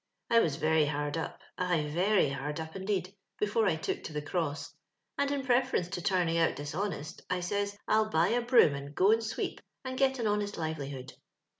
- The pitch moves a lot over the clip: Yes, wide, 5.8 semitones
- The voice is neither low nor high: Yes, medium, 180 Hz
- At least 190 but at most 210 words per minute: Yes, fast, 205 wpm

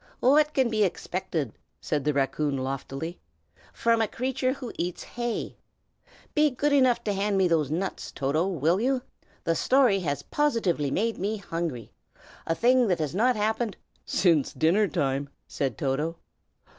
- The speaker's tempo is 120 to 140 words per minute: No, average, 155 wpm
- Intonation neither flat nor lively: No, wide, 7.7 semitones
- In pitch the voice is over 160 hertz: Yes, high, 190 Hz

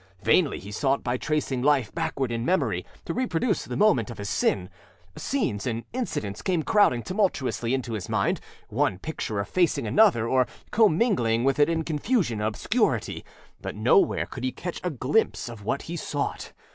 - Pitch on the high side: No, low, 135 Hz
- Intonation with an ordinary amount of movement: No, wide, 7.9 semitones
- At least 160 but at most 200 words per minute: Yes, average, 170 wpm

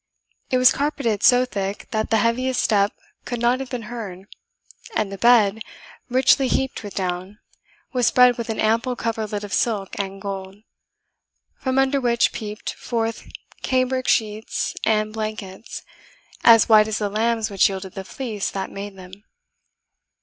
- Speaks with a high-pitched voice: Yes, high, 220 Hz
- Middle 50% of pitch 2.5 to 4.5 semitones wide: Yes, average, 3.4 semitones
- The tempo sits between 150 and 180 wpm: Yes, average, 155 wpm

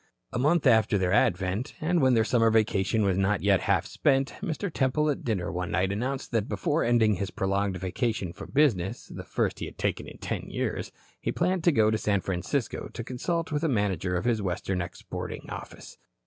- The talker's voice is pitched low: Yes, low, 110 Hz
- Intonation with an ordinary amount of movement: No, wide, 5.8 semitones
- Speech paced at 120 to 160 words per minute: No, fast, 205 wpm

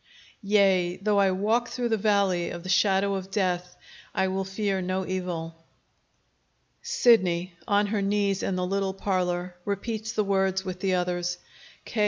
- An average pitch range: No, narrow, 1.9 semitones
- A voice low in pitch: No, high, 190 Hz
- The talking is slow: No, average, 160 wpm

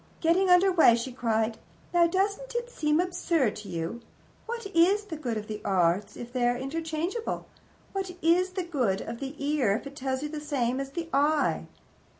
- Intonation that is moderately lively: No, wide, 6.8 semitones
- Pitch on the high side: Yes, very high, 300 Hz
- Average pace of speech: Yes, average, 190 wpm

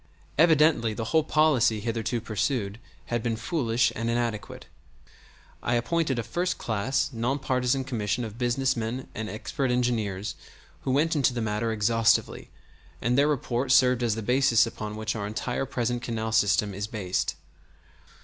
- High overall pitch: No, low, 120 Hz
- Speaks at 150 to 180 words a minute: Yes, average, 155 wpm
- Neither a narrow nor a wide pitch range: Yes, average, 3.1 semitones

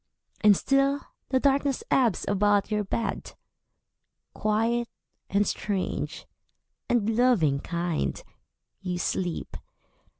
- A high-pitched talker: Yes, high, 210 Hz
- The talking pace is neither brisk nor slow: No, slow, 95 wpm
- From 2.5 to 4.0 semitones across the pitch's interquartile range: No, average, 4.5 semitones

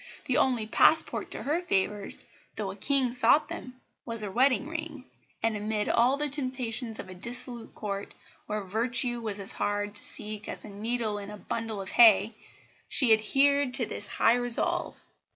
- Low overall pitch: No, high, 230 Hz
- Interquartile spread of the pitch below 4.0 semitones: Yes, average, 3.5 semitones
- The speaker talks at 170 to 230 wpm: Yes, average, 180 wpm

